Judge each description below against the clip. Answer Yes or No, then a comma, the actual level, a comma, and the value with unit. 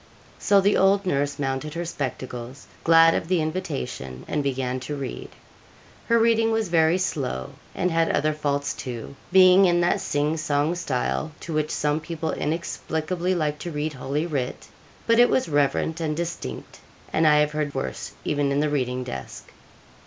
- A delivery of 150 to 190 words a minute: Yes, average, 170 wpm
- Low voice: No, medium, 155 Hz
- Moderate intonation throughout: Yes, average, 3.7 semitones